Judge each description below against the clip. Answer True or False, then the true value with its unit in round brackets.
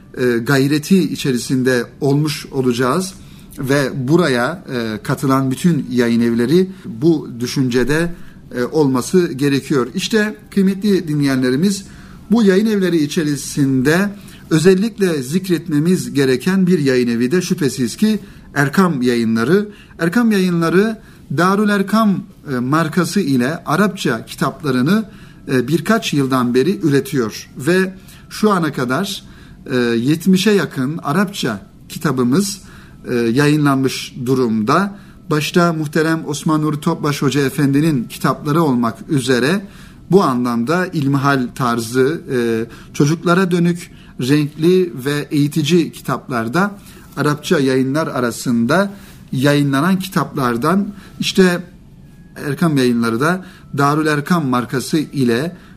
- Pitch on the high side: False (155 Hz)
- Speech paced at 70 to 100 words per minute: True (95 wpm)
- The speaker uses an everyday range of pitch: False (5.8 semitones)